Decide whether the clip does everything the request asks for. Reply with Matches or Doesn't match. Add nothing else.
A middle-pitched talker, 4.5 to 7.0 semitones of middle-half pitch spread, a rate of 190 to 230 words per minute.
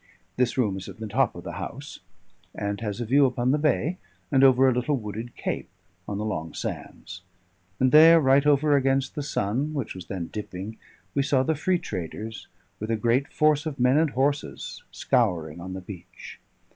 Doesn't match